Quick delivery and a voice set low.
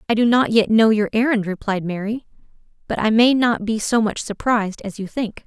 No: fast, 220 wpm; high, 220 Hz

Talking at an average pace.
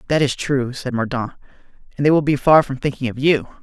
No: fast, 230 wpm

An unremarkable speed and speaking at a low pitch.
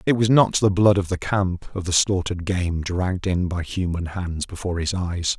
No: fast, 225 wpm; very low, 90 Hz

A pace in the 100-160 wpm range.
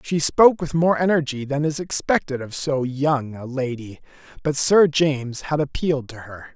No: average, 185 wpm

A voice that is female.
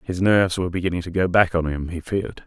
No: male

